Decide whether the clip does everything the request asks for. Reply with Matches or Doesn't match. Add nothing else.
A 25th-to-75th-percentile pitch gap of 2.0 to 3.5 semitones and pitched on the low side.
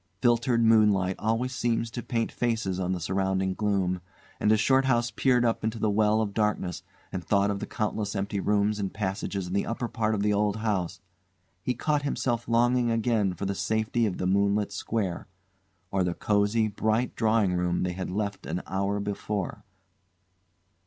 Matches